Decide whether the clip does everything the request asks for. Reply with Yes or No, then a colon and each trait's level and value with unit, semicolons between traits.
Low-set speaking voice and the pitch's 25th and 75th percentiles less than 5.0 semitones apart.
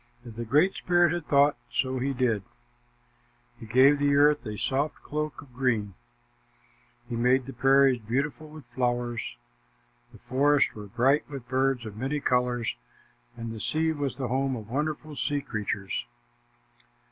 Yes: low, 130 Hz; average, 3.2 semitones